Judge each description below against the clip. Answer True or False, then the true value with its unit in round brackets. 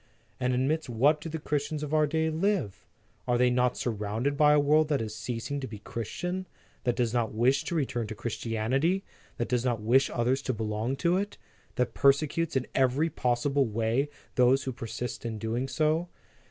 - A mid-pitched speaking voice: False (130 Hz)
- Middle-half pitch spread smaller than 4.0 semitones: False (4.3 semitones)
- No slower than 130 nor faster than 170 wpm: False (190 wpm)